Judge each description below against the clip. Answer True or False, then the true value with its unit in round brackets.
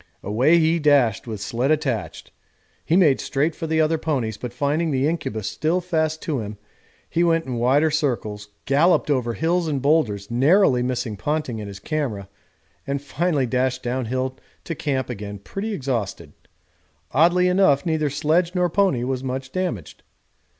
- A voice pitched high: False (140 Hz)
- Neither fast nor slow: True (165 wpm)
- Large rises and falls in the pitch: False (4.8 semitones)